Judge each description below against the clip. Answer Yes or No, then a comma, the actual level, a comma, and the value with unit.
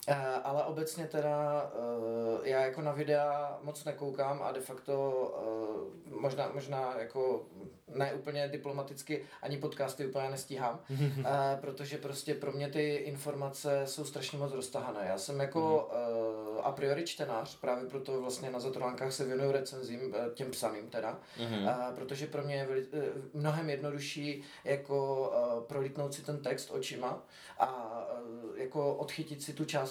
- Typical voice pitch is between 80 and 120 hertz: No, medium, 140 Hz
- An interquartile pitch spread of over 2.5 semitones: No, narrow, 1.8 semitones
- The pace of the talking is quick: No, average, 155 wpm